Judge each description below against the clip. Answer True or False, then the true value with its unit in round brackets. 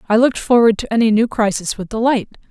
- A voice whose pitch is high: True (225 Hz)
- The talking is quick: True (215 wpm)